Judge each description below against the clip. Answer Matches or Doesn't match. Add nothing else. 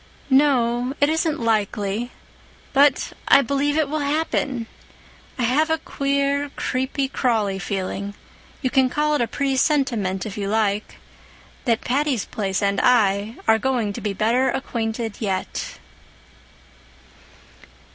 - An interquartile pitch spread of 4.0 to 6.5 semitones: Matches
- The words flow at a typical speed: Doesn't match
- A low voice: Doesn't match